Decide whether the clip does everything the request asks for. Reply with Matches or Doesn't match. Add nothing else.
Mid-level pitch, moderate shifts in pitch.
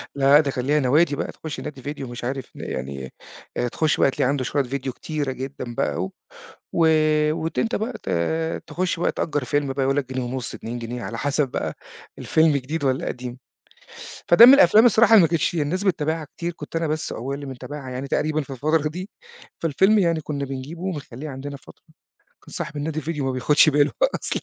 Matches